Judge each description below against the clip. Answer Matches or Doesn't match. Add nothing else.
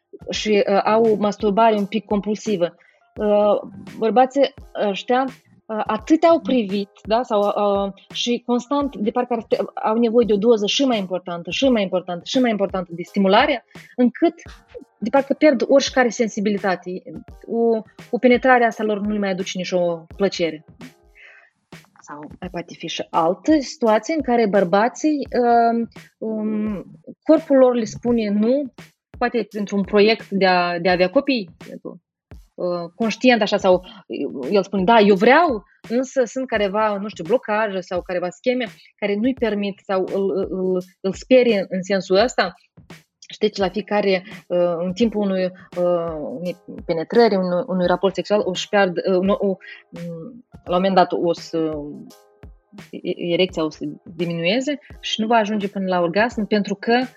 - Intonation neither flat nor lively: Matches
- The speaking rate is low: Doesn't match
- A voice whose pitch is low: Doesn't match